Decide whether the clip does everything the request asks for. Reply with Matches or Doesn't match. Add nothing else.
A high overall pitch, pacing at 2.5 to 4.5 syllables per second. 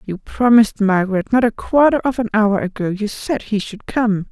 Doesn't match